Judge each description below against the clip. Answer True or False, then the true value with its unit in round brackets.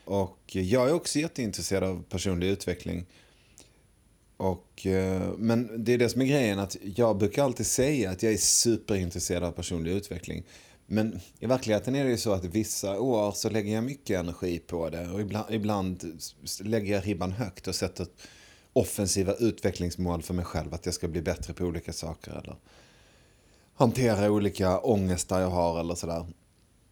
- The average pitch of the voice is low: True (95 Hz)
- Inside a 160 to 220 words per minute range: True (170 wpm)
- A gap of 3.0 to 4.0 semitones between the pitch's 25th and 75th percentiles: True (3.6 semitones)